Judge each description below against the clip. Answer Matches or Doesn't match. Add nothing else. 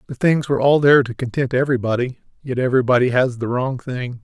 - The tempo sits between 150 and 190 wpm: Doesn't match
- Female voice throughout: Doesn't match